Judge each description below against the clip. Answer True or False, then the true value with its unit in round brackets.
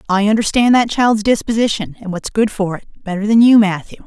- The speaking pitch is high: True (210 Hz)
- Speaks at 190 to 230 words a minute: True (205 wpm)